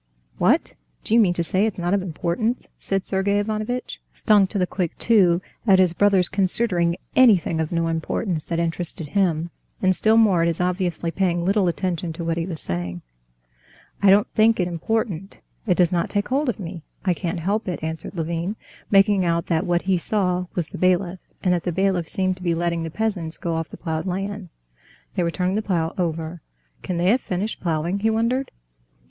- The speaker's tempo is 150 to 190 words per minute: No, average, 200 wpm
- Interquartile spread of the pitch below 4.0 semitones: Yes, average, 3.0 semitones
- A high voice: No, medium, 180 Hz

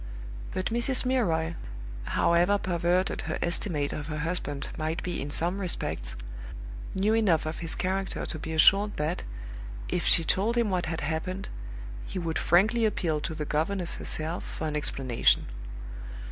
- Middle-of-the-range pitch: Yes, medium, 170 Hz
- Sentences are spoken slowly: No, average, 155 wpm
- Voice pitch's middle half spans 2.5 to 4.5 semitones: Yes, average, 3.7 semitones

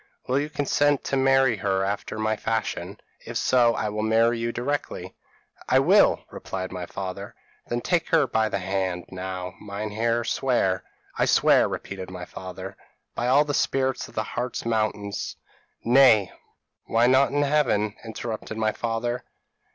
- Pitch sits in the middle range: No, low, 110 Hz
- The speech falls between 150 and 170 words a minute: Yes, average, 160 wpm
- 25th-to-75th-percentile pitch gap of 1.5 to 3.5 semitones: No, average, 4.5 semitones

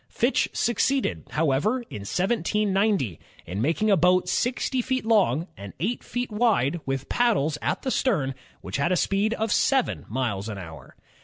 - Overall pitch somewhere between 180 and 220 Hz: Yes, medium, 185 Hz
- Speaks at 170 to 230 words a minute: No, average, 160 wpm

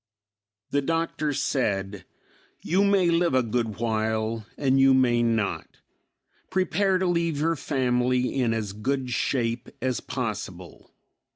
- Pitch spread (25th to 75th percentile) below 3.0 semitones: No, average, 5.0 semitones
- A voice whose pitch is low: Yes, low, 125 Hz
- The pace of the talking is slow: Yes, slow, 125 wpm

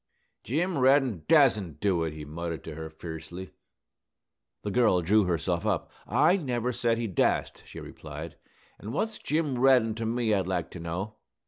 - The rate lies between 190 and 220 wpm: No, average, 165 wpm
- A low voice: Yes, low, 105 Hz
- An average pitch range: No, wide, 6.6 semitones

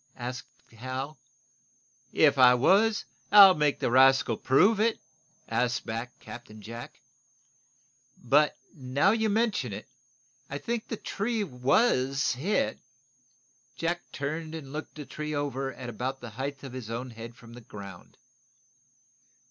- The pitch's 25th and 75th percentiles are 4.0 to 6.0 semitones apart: Yes, average, 4.7 semitones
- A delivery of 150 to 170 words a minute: No, average, 140 wpm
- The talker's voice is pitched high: No, low, 135 Hz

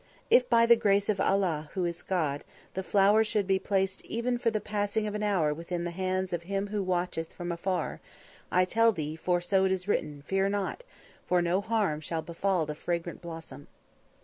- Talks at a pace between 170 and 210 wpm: Yes, average, 200 wpm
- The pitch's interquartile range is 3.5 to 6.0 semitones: No, average, 3.1 semitones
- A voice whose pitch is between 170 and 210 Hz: Yes, high, 190 Hz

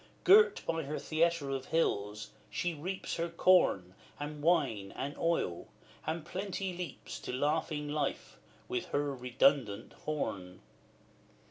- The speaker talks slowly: Yes, slow, 125 wpm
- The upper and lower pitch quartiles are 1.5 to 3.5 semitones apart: No, average, 4.3 semitones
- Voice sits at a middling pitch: Yes, medium, 150 Hz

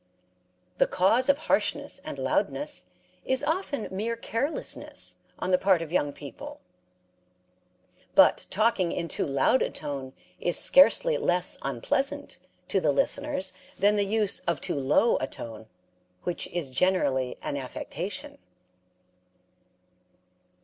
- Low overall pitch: No, medium, 185 Hz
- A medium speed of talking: No, slow, 125 wpm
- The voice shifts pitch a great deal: Yes, wide, 8.3 semitones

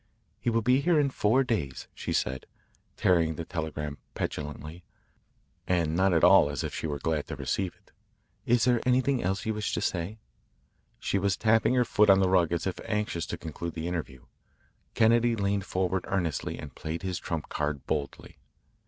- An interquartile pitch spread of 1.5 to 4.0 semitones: No, wide, 5.5 semitones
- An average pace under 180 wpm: No, average, 190 wpm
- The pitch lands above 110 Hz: No, very low, 95 Hz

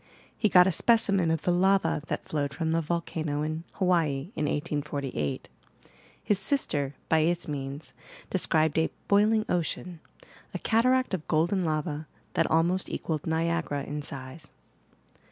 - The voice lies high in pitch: No, medium, 160 Hz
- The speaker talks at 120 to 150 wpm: Yes, average, 140 wpm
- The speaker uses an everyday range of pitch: Yes, average, 3.6 semitones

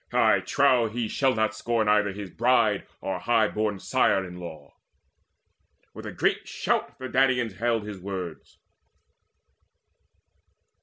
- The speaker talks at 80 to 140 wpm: Yes, slow, 135 wpm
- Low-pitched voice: Yes, low, 110 Hz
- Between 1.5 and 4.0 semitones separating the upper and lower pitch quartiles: Yes, average, 3.3 semitones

